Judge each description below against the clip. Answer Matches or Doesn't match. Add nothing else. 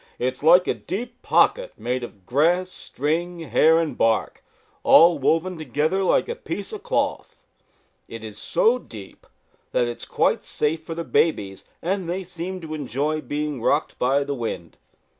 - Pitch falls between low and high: Matches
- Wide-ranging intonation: Matches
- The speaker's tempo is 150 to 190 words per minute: Matches